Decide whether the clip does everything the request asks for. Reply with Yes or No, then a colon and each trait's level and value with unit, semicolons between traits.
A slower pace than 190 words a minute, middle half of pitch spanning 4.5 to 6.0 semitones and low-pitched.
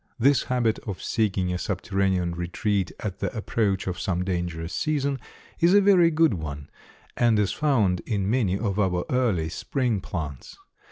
Yes: average, 160 wpm; wide, 5.4 semitones; low, 100 Hz